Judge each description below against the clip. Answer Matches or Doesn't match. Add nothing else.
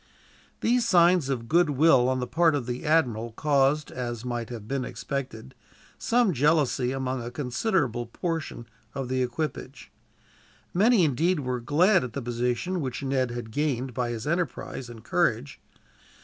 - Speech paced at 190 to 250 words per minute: Doesn't match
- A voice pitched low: Matches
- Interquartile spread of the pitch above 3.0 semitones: Matches